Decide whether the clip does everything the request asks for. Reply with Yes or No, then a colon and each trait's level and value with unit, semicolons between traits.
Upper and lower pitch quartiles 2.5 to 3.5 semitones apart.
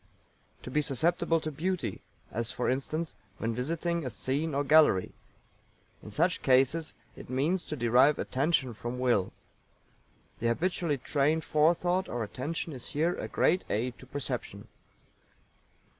No: average, 4.6 semitones